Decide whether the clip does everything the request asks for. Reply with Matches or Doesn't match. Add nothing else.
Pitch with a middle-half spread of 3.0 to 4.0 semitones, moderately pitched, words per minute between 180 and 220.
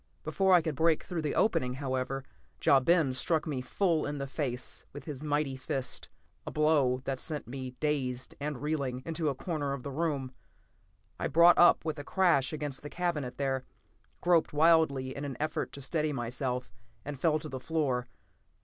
Matches